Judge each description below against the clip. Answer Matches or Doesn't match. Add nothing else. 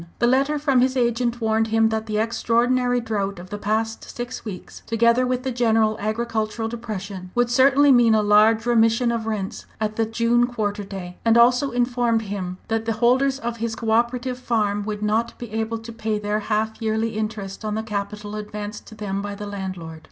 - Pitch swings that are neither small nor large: Doesn't match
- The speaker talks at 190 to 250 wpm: Matches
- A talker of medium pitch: Doesn't match